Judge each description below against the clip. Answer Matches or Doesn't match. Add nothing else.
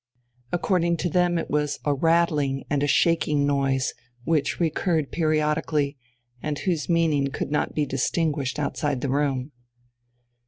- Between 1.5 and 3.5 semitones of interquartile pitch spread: Matches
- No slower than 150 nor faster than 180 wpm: Doesn't match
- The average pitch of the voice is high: Doesn't match